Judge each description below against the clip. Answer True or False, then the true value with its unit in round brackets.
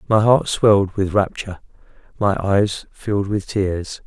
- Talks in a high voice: False (100 Hz)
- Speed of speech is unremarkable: True (150 wpm)